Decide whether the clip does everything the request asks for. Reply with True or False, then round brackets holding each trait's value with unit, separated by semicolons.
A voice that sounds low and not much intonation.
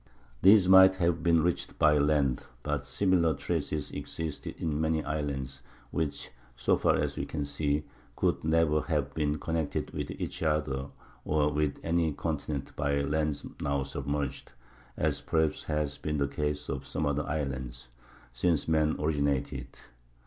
True (75 Hz; 2.1 semitones)